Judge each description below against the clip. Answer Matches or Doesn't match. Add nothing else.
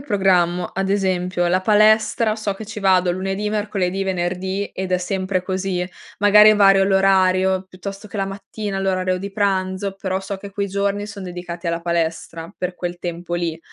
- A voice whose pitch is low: Doesn't match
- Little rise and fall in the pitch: Matches